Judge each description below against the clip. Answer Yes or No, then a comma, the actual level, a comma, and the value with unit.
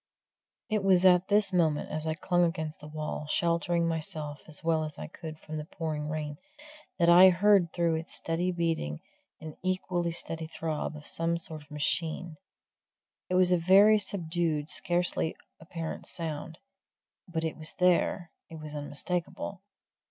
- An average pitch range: No, narrow, 2.3 semitones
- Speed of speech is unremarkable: Yes, average, 160 wpm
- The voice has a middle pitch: Yes, medium, 165 Hz